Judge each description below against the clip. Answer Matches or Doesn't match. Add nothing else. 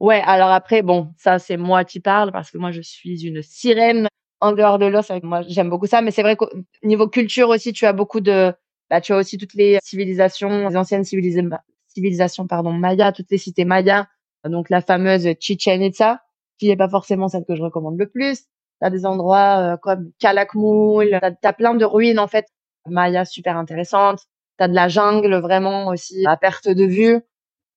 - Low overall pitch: Doesn't match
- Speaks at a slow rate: Doesn't match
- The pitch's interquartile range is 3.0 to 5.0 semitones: Doesn't match